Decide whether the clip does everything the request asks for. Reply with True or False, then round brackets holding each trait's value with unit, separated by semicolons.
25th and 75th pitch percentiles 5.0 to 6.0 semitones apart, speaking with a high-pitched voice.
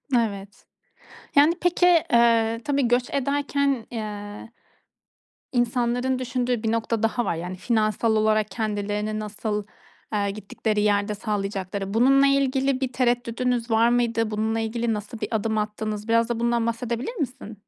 False (2.6 semitones; 230 Hz)